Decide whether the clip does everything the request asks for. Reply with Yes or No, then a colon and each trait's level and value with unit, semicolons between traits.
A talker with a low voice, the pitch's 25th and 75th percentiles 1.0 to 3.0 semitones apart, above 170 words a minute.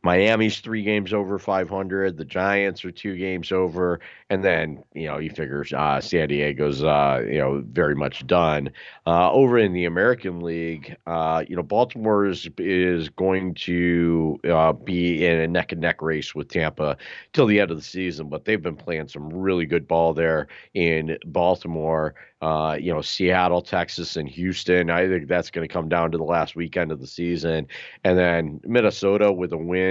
Yes: very low, 85 Hz; narrow, 2.5 semitones; average, 190 wpm